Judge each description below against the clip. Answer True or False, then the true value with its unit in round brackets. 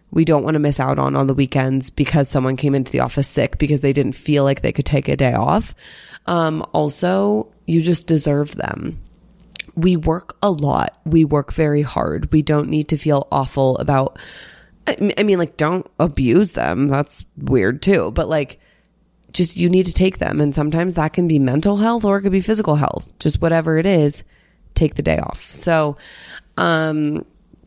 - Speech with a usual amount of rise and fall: True (3.8 semitones)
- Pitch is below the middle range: False (150 Hz)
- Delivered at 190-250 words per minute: True (195 wpm)